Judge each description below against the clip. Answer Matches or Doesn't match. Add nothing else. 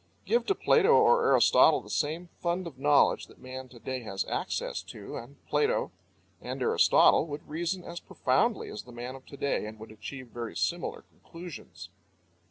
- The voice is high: Doesn't match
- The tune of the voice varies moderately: Doesn't match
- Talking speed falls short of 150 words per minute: Doesn't match